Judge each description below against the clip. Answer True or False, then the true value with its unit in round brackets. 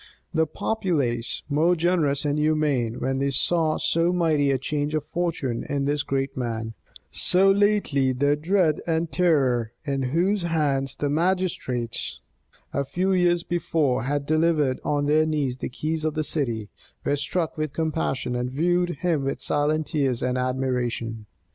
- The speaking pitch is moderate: True (150 Hz)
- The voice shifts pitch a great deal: False (3.9 semitones)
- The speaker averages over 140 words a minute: True (155 wpm)